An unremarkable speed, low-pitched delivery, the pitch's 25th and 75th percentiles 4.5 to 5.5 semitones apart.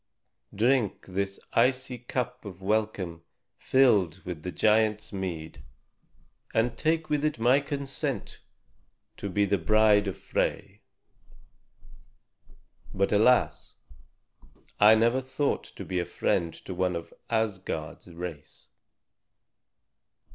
No: slow, 110 wpm; low, 105 Hz; average, 5.1 semitones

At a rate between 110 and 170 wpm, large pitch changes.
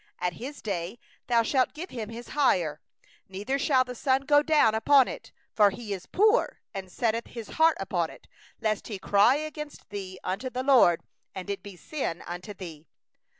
No: average, 190 wpm; wide, 6.1 semitones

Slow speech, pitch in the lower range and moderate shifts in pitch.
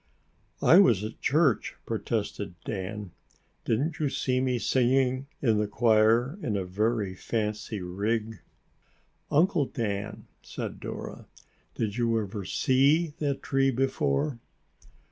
Yes: slow, 120 wpm; low, 115 Hz; average, 4.3 semitones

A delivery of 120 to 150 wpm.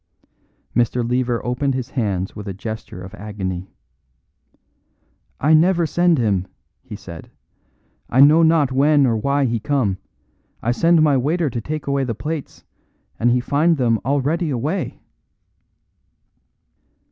Yes: slow, 135 wpm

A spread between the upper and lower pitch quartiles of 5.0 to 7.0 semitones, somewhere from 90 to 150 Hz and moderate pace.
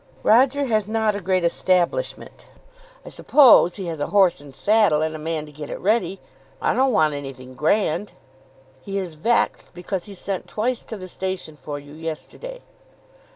No: wide, 5.6 semitones; medium, 185 Hz; average, 175 wpm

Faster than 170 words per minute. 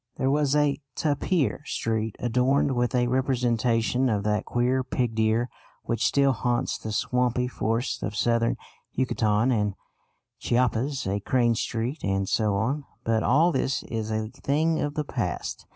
No: average, 150 wpm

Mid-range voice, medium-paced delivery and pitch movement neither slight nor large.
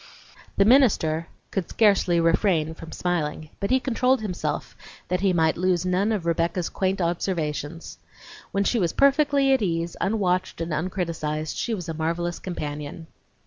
Yes: medium, 175 Hz; average, 150 wpm; average, 3.4 semitones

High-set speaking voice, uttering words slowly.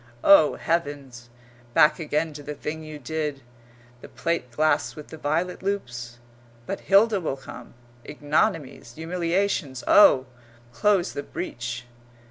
No: medium, 155 Hz; slow, 125 wpm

